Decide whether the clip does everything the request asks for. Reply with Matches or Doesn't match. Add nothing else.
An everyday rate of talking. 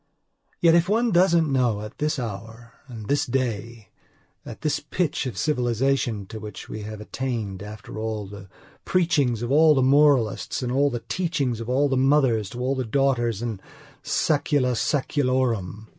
Matches